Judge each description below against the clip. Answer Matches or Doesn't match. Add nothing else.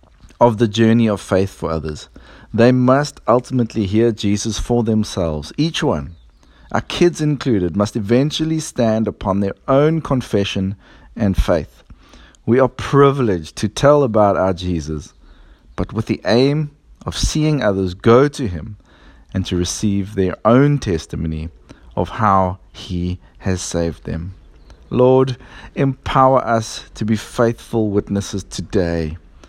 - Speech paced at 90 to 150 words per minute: Matches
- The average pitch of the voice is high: Doesn't match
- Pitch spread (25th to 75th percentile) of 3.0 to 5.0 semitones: Doesn't match